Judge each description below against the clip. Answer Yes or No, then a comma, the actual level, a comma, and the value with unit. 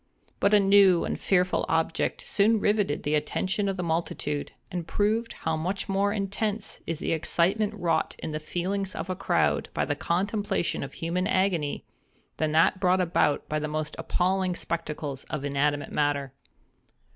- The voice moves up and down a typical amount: Yes, average, 4.2 semitones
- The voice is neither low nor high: Yes, medium, 180 Hz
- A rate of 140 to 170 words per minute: Yes, average, 165 wpm